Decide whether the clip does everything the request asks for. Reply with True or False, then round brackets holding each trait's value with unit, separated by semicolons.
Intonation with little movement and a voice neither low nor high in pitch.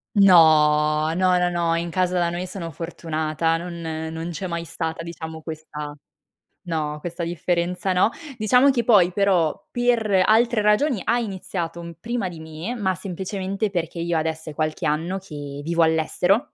False (3.2 semitones; 170 Hz)